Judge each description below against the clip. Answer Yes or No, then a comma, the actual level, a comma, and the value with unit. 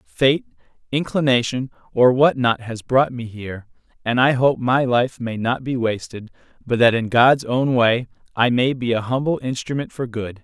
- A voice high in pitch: No, low, 125 Hz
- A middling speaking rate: Yes, average, 185 wpm